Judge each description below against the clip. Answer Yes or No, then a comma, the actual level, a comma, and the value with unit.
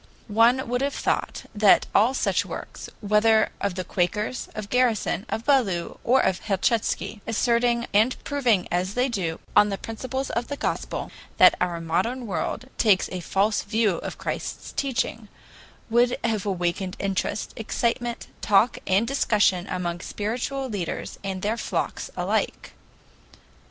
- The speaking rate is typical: Yes, average, 145 wpm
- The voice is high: Yes, high, 215 Hz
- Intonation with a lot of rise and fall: No, average, 3.9 semitones